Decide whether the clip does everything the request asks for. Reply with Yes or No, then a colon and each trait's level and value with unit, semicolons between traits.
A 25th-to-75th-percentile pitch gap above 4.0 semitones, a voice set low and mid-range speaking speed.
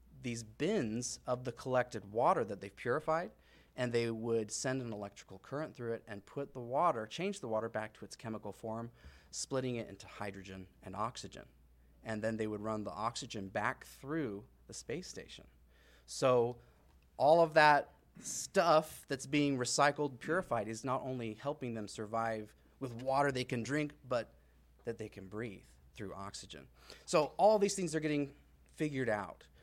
Yes: average, 4.7 semitones; low, 115 Hz; average, 170 wpm